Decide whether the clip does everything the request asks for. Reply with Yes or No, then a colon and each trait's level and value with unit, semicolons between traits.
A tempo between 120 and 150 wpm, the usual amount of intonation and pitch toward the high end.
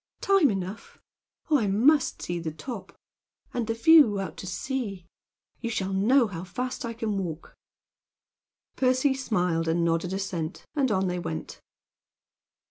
No: average, 145 wpm; wide, 6.0 semitones; high, 200 Hz